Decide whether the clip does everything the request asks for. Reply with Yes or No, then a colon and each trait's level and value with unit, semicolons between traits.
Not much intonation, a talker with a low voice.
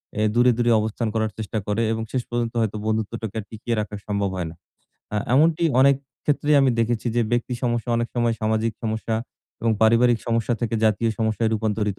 Yes: narrow, 1.7 semitones; low, 115 Hz